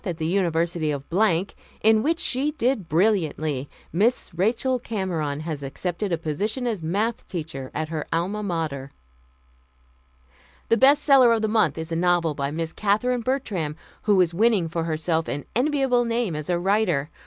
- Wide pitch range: Yes, wide, 5.9 semitones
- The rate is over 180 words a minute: No, average, 165 wpm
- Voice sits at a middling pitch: Yes, medium, 180 Hz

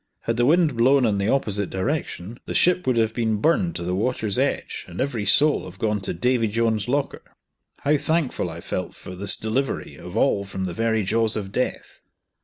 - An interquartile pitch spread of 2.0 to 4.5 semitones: No, average, 5.0 semitones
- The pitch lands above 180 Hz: No, low, 115 Hz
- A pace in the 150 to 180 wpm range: No, fast, 205 wpm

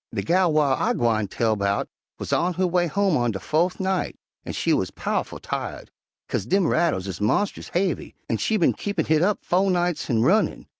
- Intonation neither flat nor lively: No, wide, 8.0 semitones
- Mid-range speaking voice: Yes, medium, 170 Hz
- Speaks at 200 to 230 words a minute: Yes, fast, 205 wpm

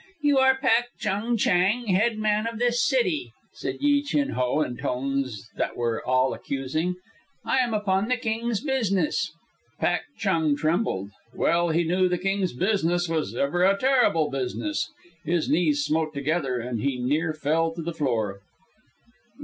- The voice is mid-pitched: Yes, medium, 175 Hz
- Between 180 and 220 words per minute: No, average, 160 wpm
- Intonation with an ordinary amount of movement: No, wide, 7.7 semitones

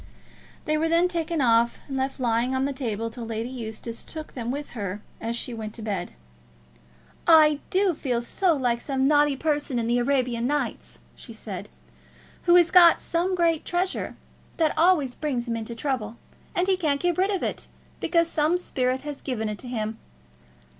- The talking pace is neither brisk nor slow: Yes, average, 185 wpm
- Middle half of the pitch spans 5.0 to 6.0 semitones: Yes, wide, 5.6 semitones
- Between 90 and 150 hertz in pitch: No, very high, 270 Hz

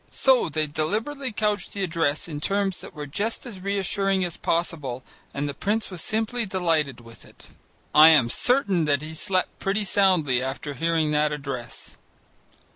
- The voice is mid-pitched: Yes, medium, 170 Hz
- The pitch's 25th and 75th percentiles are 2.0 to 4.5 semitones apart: No, average, 5.3 semitones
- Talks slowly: No, average, 165 wpm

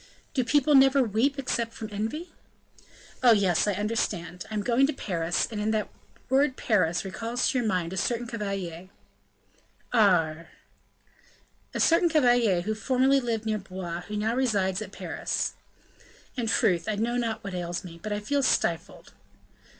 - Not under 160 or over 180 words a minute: Yes, average, 165 wpm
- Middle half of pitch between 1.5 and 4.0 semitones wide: No, average, 4.8 semitones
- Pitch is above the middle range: Yes, high, 215 Hz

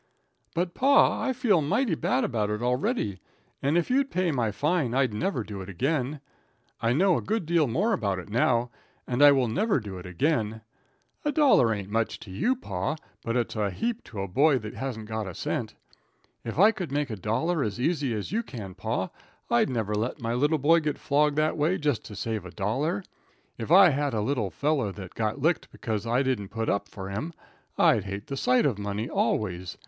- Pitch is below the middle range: Yes, low, 125 Hz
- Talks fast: Yes, fast, 210 wpm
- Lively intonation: Yes, wide, 6.7 semitones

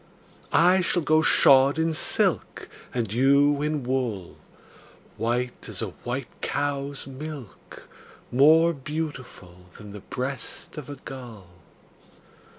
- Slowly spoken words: Yes, slow, 115 wpm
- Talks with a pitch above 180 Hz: No, low, 135 Hz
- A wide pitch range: No, average, 3.8 semitones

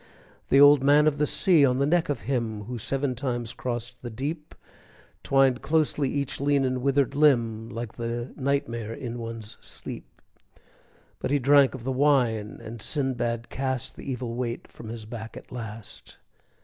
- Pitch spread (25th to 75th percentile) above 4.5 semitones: No, average, 3.2 semitones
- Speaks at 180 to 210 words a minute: No, average, 170 wpm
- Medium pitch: No, low, 130 Hz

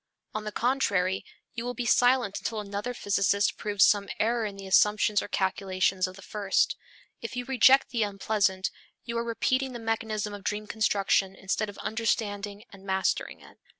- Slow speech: No, average, 175 wpm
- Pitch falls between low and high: No, high, 210 Hz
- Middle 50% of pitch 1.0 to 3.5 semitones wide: Yes, narrow, 2.6 semitones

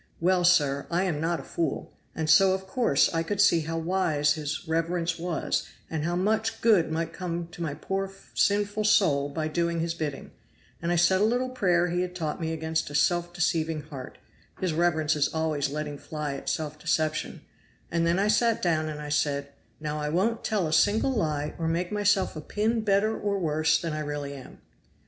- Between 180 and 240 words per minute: Yes, fast, 205 wpm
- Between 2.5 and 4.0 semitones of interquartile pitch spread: Yes, average, 3.6 semitones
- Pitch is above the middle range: No, medium, 165 Hz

